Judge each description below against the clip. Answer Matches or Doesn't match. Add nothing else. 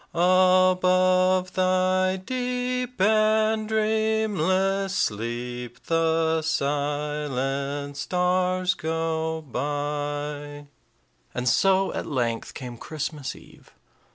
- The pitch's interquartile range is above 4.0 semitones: Matches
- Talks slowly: Matches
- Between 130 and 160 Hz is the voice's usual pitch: Doesn't match